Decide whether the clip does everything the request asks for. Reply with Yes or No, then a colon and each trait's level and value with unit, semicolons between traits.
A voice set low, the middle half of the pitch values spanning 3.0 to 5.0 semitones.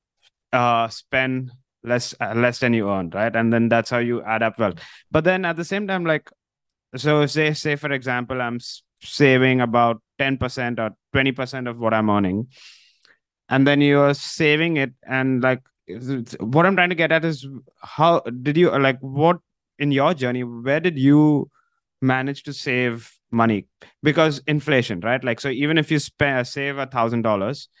Yes: low, 130 Hz; average, 3.7 semitones